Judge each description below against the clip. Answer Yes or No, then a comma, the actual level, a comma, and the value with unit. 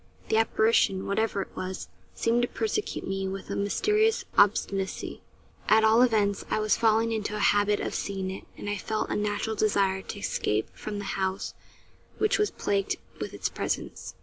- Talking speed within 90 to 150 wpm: No, average, 175 wpm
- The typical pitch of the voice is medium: No, high, 205 Hz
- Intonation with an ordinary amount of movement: No, narrow, 2.3 semitones